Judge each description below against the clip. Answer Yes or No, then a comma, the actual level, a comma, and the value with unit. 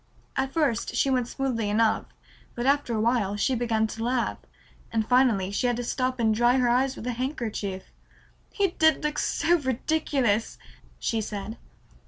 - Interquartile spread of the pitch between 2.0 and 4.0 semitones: Yes, average, 3.2 semitones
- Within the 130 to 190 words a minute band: Yes, average, 170 wpm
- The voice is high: Yes, high, 245 Hz